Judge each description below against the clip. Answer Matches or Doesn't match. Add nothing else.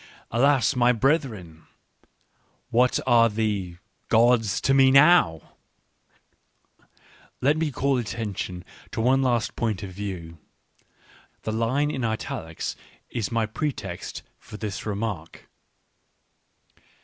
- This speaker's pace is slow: Matches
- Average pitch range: Matches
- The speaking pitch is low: Matches